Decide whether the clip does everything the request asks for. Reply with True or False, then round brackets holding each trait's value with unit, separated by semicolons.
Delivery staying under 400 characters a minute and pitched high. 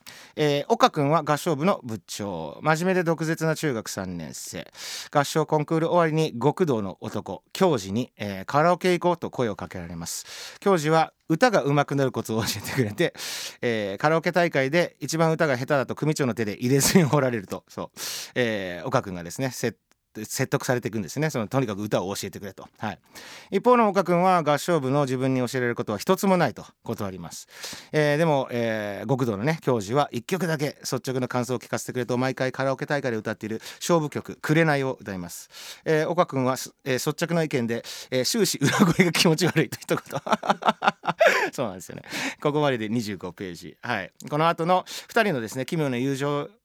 False (375 characters per minute; 140 Hz)